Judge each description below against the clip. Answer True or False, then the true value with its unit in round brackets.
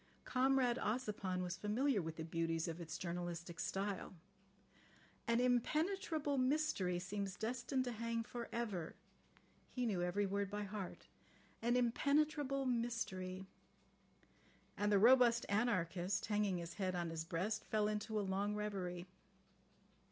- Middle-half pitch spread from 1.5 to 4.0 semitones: False (4.9 semitones)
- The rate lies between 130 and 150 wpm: True (135 wpm)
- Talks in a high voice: True (210 Hz)